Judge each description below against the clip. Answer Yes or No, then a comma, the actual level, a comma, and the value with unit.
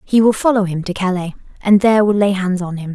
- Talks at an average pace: No, fast, 265 wpm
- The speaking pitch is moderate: No, high, 195 Hz